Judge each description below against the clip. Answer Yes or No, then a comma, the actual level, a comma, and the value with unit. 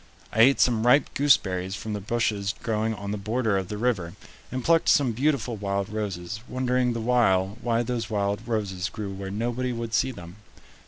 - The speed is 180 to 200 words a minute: Yes, average, 190 wpm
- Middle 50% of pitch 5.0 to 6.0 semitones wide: No, average, 3.5 semitones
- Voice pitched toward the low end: Yes, low, 110 Hz